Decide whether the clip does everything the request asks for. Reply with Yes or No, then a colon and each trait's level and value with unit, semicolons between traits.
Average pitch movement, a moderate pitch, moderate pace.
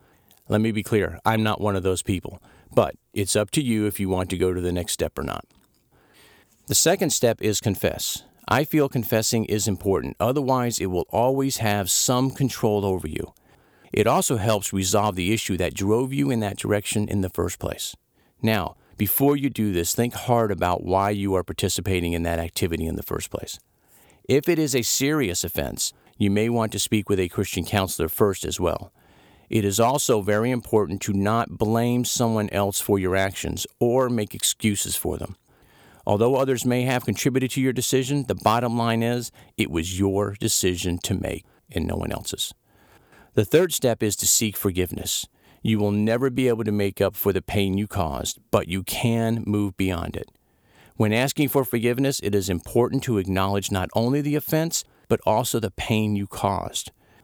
No: average, 3.7 semitones; low, 105 Hz; average, 190 wpm